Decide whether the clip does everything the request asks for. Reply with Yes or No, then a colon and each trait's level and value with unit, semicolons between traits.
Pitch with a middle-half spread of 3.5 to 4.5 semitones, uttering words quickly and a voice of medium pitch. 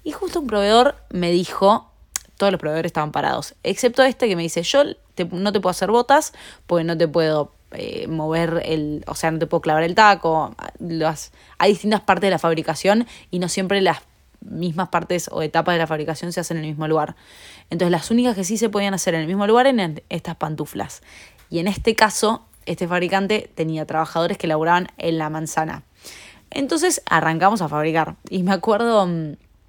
Yes: average, 4.2 semitones; fast, 195 wpm; medium, 175 Hz